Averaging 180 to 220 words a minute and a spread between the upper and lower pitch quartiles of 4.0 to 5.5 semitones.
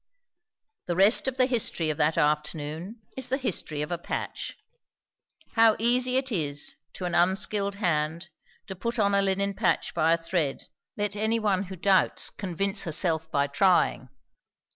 No: average, 160 wpm; average, 4.7 semitones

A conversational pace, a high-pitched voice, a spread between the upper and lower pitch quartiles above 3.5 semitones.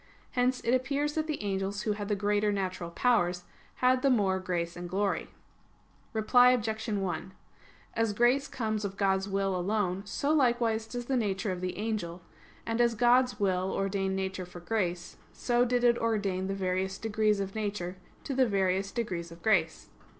Yes: average, 175 wpm; high, 205 Hz; average, 3.9 semitones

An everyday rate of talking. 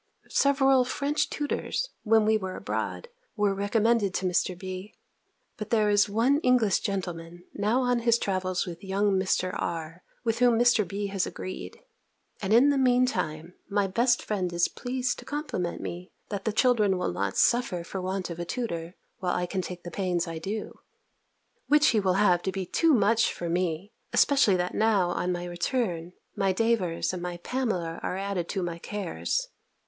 Yes: average, 180 wpm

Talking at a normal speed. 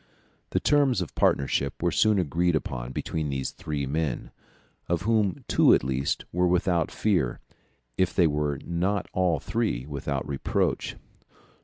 Yes: average, 145 wpm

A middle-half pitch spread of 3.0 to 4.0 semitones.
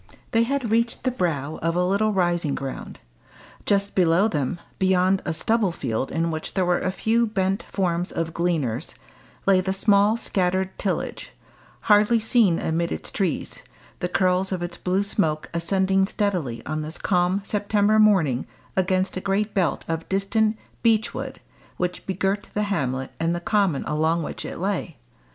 Yes: average, 3.4 semitones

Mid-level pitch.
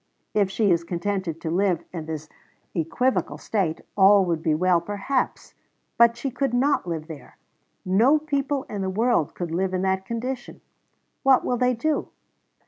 No: high, 195 Hz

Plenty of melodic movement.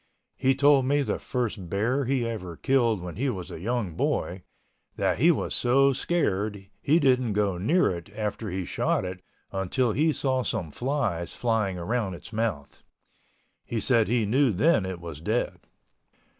Yes: wide, 5.8 semitones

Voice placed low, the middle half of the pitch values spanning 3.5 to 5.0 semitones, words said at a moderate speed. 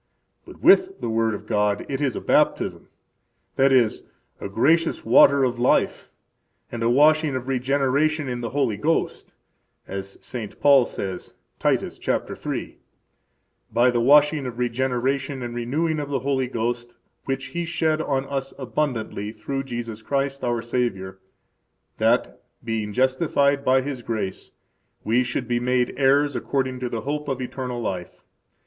No: low, 130 Hz; average, 3.1 semitones; average, 155 wpm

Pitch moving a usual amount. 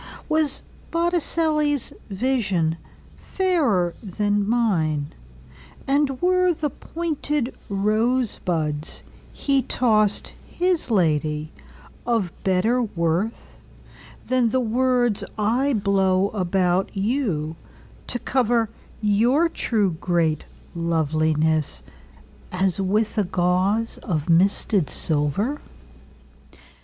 No: wide, 7.2 semitones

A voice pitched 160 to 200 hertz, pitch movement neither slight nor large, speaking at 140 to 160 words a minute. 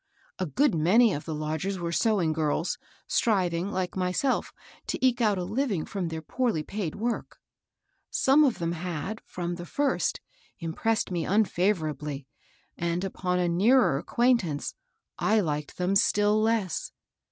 Yes: medium, 185 Hz; average, 4.7 semitones; average, 145 wpm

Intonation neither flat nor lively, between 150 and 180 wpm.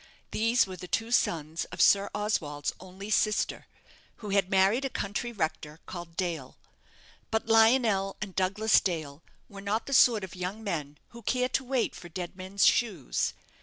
Yes: average, 4.1 semitones; average, 165 wpm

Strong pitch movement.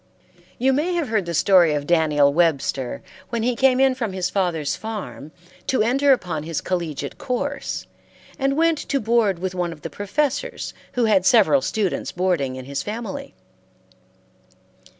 Yes: wide, 7.7 semitones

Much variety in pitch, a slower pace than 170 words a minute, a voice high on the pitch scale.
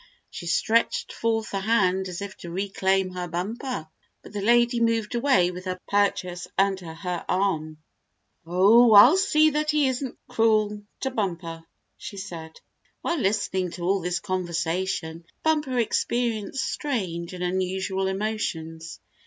No: average, 4.3 semitones; average, 140 wpm; high, 195 Hz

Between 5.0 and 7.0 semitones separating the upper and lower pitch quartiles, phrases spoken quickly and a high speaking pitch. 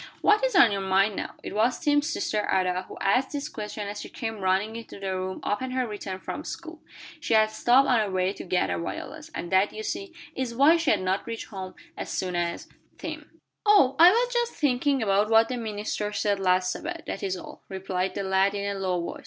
Yes: wide, 5.6 semitones; fast, 225 wpm; high, 210 Hz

